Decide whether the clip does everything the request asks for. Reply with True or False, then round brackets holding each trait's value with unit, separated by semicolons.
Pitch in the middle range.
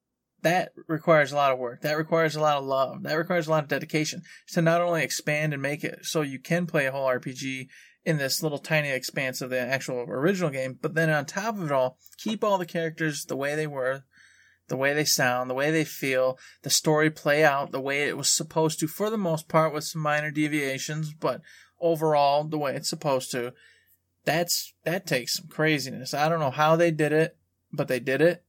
True (150 Hz)